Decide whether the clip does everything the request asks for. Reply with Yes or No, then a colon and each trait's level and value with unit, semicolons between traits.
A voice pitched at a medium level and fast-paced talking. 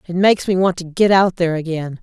Yes: medium, 175 Hz; fast, 265 wpm